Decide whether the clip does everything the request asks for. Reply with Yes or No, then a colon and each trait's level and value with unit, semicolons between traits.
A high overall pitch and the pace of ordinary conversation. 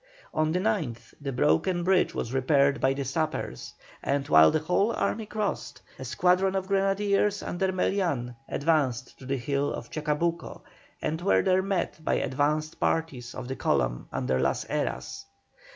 No: medium, 155 Hz; average, 160 wpm